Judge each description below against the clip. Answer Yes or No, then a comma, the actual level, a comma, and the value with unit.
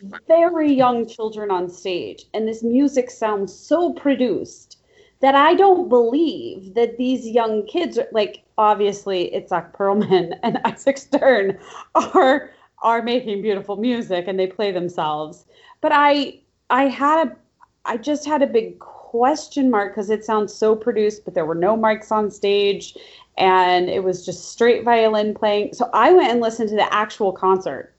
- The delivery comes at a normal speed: Yes, average, 165 wpm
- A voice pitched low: No, high, 225 Hz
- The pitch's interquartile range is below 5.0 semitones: No, average, 5.3 semitones